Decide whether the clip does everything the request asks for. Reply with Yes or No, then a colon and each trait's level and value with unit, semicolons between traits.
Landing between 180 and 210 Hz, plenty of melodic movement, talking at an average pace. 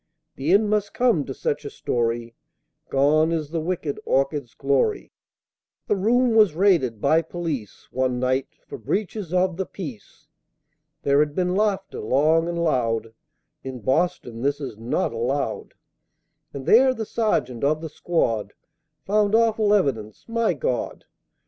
No: medium, 155 Hz; wide, 7.0 semitones; average, 145 wpm